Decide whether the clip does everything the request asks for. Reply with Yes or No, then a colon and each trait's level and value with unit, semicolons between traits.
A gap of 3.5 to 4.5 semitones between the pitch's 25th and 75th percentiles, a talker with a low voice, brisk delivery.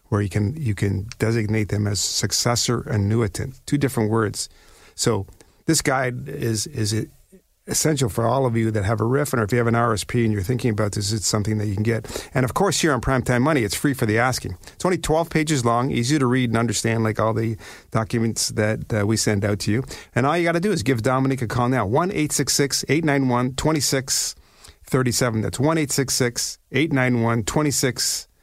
Yes: average, 4.0 semitones; low, 120 Hz; fast, 235 wpm